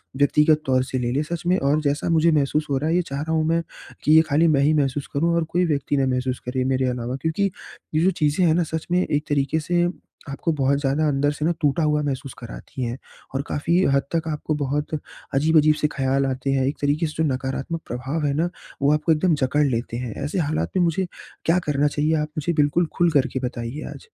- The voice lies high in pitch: No, medium, 150 Hz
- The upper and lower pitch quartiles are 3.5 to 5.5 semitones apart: No, average, 2.7 semitones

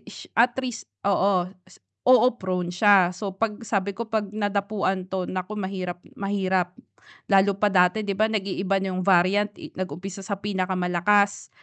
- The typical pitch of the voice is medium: No, high, 195 Hz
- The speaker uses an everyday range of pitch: No, narrow, 2.0 semitones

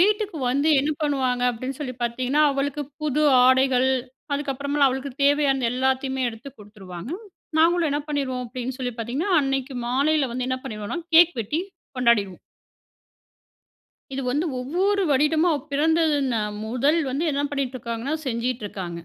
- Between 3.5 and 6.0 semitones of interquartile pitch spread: No, average, 2.9 semitones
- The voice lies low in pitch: No, very high, 265 Hz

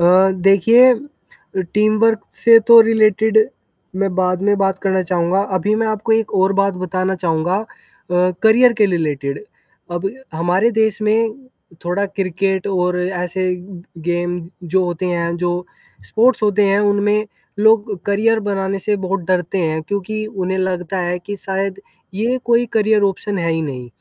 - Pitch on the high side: Yes, high, 195 Hz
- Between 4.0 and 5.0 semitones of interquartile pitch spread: No, average, 3.1 semitones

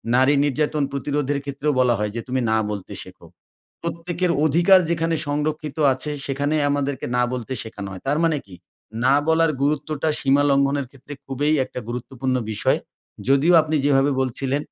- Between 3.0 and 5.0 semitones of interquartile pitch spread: No, narrow, 2.6 semitones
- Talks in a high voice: No, medium, 140 Hz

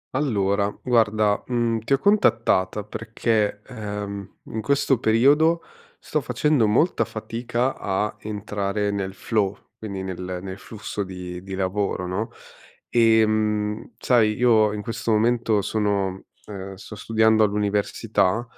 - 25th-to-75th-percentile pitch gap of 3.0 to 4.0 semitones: No, narrow, 2.4 semitones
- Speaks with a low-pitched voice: Yes, low, 105 Hz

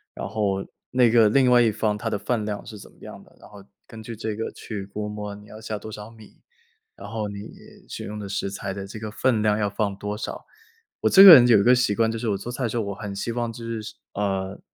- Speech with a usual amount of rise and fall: No, narrow, 2.0 semitones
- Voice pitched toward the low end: Yes, low, 105 Hz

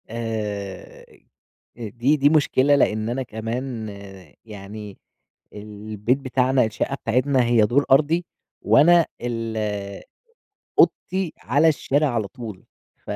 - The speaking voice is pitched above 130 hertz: No, low, 120 Hz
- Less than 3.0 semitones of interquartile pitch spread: No, average, 4.2 semitones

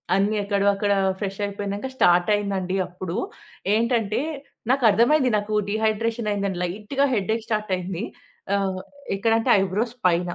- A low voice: No, high, 205 Hz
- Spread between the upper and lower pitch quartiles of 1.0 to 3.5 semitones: Yes, narrow, 2.5 semitones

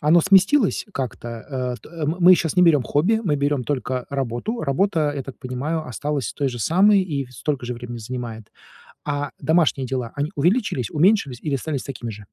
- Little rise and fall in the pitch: No, average, 4.7 semitones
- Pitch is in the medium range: Yes, medium, 145 Hz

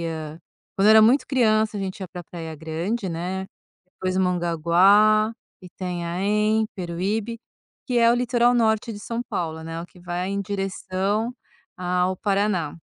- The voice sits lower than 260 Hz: Yes, high, 190 Hz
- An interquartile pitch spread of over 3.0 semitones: Yes, average, 3.5 semitones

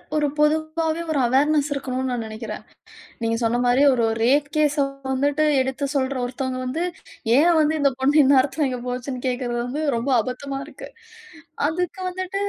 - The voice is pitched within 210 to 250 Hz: No, very high, 275 Hz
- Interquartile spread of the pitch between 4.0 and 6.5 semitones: No, average, 3.3 semitones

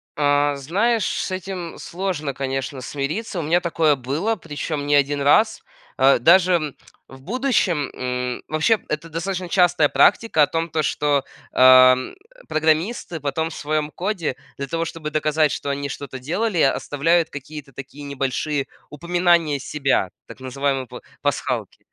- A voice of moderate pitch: Yes, medium, 150 Hz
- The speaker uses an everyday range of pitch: Yes, average, 3.8 semitones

